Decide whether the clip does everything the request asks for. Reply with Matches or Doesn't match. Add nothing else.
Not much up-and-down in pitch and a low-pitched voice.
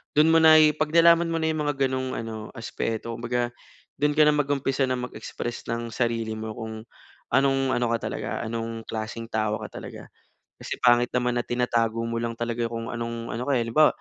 Doesn't match